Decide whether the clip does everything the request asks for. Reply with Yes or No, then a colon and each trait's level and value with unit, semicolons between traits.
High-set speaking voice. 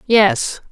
Yes: high, 220 Hz